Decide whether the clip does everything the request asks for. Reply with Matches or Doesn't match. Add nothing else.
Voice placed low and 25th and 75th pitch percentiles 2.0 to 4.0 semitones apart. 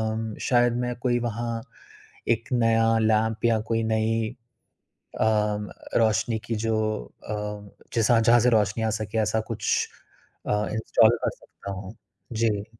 Doesn't match